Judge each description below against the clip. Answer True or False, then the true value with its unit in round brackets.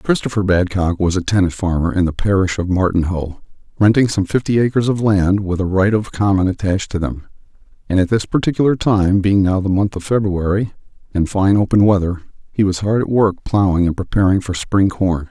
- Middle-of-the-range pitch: False (95 Hz)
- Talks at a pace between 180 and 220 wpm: True (200 wpm)